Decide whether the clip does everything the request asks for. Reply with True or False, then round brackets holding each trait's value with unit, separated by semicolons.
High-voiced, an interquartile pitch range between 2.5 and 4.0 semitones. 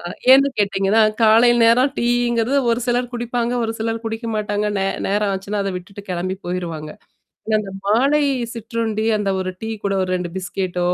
True (215 Hz; 3.3 semitones)